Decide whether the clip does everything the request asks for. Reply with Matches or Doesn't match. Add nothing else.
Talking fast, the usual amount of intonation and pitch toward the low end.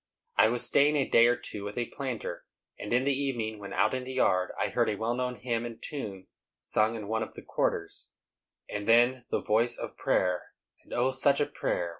Matches